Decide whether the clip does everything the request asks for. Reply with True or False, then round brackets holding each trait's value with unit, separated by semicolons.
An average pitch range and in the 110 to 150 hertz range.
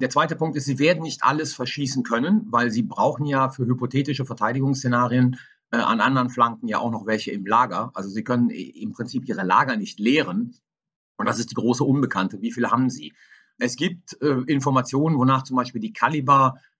True (3.1 semitones; 130 Hz)